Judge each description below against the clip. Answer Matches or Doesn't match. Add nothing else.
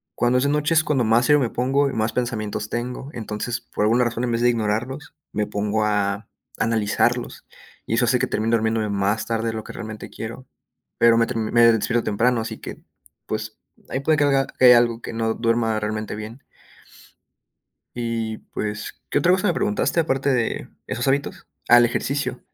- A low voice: Matches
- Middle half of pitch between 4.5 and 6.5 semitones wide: Doesn't match